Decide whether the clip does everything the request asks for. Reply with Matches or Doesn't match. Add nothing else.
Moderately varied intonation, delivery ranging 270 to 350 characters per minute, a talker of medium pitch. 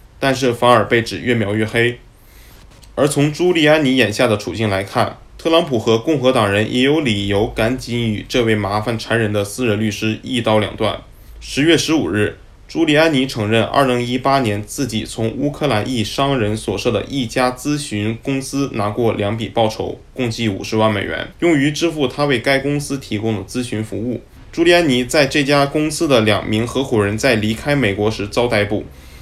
Doesn't match